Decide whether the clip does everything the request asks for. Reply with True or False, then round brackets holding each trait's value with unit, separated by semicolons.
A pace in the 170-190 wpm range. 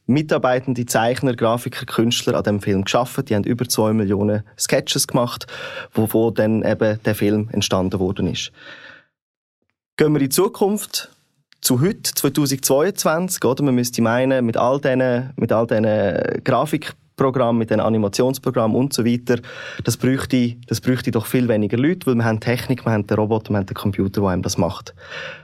False (160 wpm)